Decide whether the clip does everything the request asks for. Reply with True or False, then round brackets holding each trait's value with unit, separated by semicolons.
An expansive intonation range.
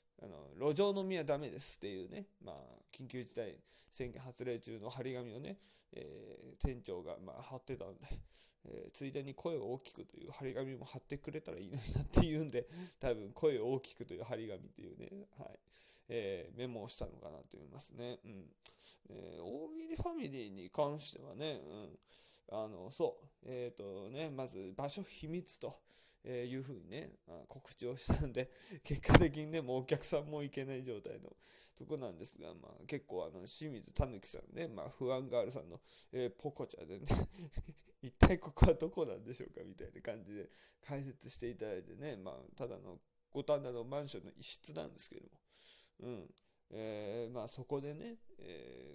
False (4.4 semitones)